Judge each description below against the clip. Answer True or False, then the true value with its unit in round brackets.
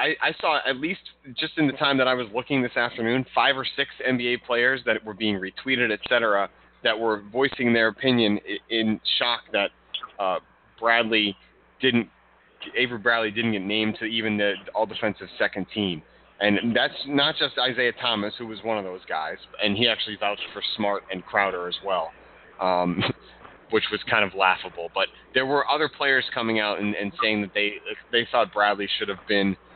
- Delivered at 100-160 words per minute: False (190 wpm)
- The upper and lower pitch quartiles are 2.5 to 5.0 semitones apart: True (3.0 semitones)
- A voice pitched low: True (110 Hz)